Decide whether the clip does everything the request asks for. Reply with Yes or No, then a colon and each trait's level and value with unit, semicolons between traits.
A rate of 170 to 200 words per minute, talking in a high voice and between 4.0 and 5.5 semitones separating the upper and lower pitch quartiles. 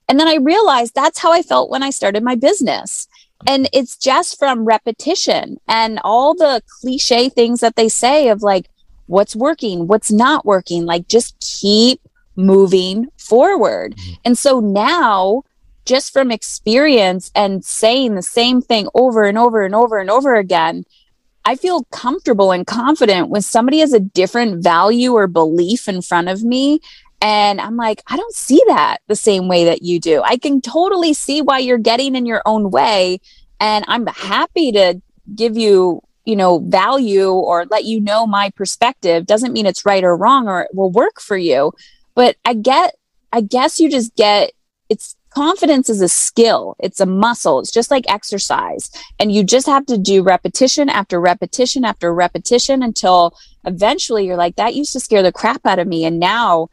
Yes: average, 180 wpm; high, 225 Hz; average, 5.2 semitones